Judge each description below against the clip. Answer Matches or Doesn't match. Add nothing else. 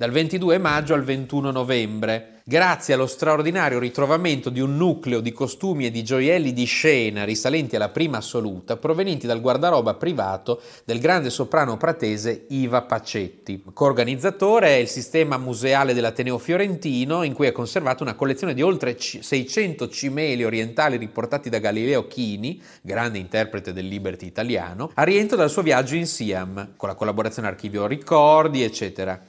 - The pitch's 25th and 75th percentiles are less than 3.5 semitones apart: Doesn't match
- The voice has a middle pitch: Doesn't match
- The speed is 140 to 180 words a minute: Matches